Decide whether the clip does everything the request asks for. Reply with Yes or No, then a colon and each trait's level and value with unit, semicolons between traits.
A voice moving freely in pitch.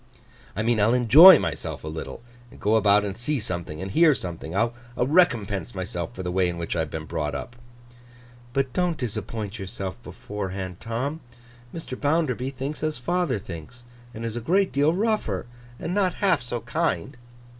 Yes: wide, 7.4 semitones